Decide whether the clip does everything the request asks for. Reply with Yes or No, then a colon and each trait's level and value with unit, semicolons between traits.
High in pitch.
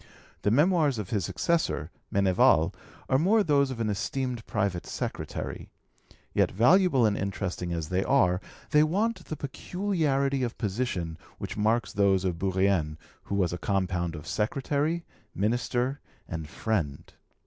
No: low, 110 Hz